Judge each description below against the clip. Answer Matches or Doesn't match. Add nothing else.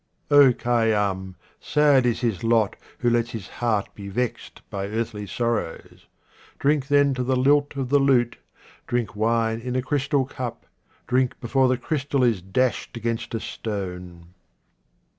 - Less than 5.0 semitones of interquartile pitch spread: Matches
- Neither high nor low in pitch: Doesn't match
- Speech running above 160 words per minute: Doesn't match